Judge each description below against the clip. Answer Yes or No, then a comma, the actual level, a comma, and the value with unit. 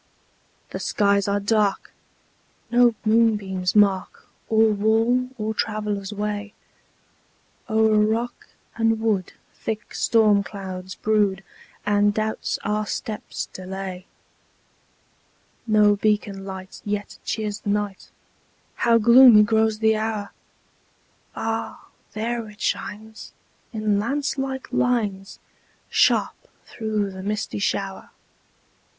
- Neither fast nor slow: No, slow, 105 wpm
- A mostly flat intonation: Yes, narrow, 1.6 semitones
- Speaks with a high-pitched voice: Yes, high, 210 Hz